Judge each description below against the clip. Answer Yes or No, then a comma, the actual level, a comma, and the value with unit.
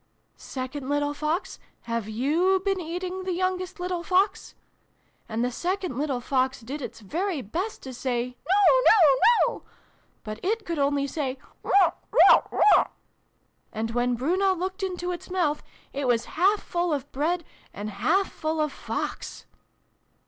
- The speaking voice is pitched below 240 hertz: No, very high, 310 Hz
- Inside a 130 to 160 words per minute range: Yes, average, 155 wpm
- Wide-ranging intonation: Yes, wide, 6.2 semitones